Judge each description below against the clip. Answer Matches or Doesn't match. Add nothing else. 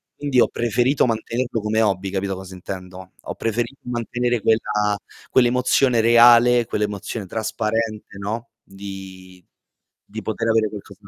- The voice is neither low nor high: Doesn't match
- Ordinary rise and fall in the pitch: Matches